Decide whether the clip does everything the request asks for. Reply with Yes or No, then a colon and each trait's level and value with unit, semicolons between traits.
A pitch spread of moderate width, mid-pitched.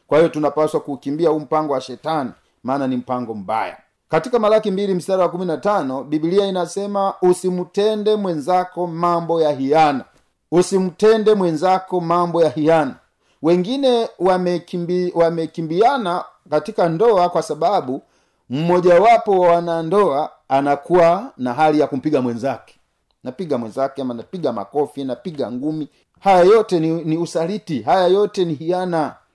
Yes: average, 3.5 semitones; medium, 170 Hz